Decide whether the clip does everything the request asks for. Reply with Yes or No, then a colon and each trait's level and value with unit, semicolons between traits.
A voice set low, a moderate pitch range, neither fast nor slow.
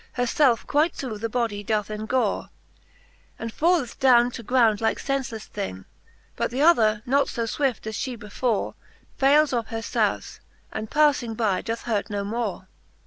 No: high, 235 Hz; average, 3.5 semitones; average, 165 wpm